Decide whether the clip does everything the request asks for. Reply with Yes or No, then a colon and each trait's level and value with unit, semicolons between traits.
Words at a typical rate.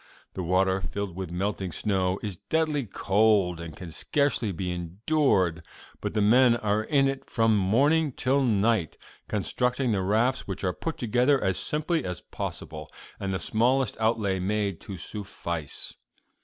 Yes: average, 155 wpm